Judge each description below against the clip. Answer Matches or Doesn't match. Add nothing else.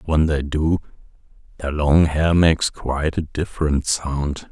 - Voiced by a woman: Doesn't match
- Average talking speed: Matches